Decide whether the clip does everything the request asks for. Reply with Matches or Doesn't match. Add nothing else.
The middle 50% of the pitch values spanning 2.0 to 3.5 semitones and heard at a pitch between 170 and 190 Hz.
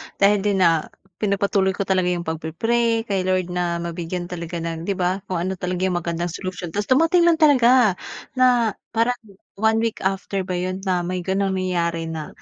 Matches